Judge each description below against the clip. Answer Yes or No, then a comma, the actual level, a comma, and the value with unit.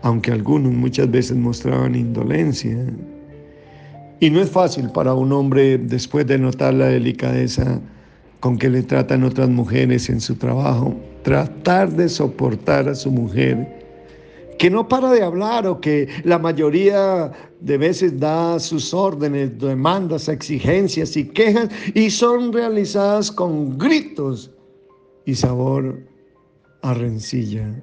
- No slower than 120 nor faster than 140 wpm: Yes, average, 130 wpm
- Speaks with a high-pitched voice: No, medium, 140 Hz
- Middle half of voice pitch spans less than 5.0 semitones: No, wide, 5.6 semitones